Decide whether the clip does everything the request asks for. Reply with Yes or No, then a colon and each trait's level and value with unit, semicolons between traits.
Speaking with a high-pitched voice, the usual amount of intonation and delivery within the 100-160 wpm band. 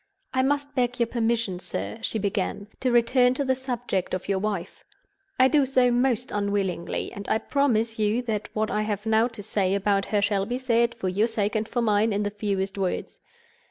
No: high, 220 Hz; average, 3.4 semitones; fast, 205 wpm